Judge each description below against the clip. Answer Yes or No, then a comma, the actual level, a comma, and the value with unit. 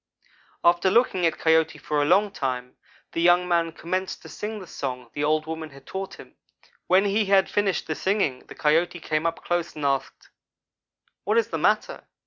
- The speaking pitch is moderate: Yes, medium, 170 Hz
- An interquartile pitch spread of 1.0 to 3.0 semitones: No, average, 3.8 semitones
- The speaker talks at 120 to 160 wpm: No, average, 190 wpm